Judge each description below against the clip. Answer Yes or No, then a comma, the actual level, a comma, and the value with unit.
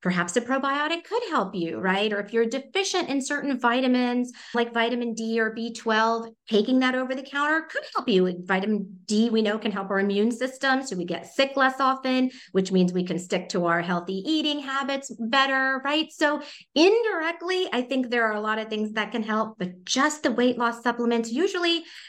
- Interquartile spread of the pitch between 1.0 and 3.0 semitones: No, average, 4.5 semitones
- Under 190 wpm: No, average, 200 wpm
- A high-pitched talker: Yes, high, 240 Hz